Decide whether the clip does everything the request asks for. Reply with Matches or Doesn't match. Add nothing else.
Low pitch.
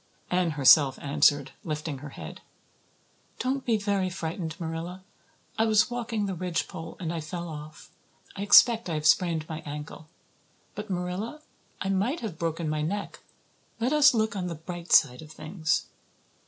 Doesn't match